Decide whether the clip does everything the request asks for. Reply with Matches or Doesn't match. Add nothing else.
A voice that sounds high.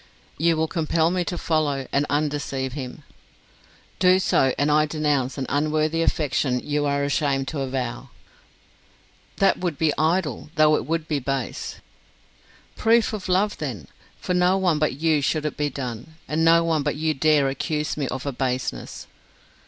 Doesn't match